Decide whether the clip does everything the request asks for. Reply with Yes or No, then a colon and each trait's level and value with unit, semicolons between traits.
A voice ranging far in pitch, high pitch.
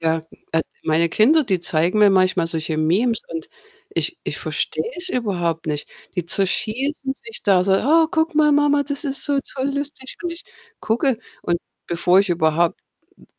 Yes: wide, 9.0 semitones; high, 205 Hz